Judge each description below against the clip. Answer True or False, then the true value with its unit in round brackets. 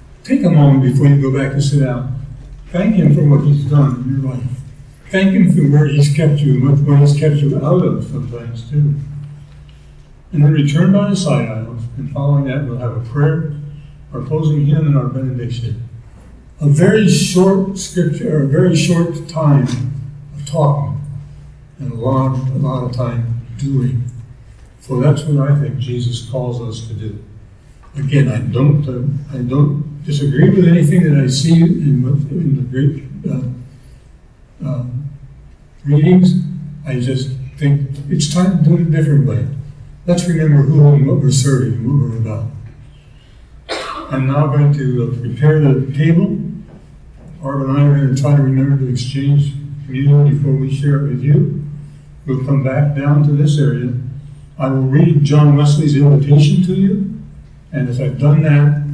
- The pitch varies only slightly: True (2.2 semitones)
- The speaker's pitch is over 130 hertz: True (140 Hz)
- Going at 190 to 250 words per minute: False (170 wpm)